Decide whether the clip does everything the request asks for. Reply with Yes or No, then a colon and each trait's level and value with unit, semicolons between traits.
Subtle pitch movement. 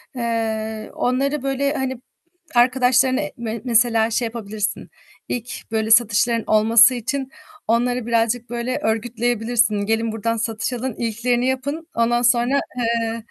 Yes: narrow, 1.9 semitones